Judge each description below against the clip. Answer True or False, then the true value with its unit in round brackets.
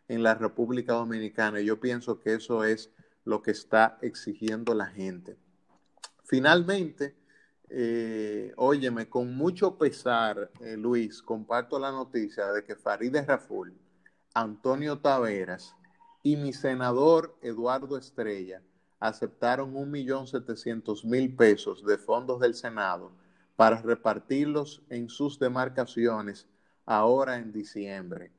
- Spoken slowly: True (115 wpm)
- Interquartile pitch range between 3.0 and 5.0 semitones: True (3.6 semitones)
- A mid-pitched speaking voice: False (115 Hz)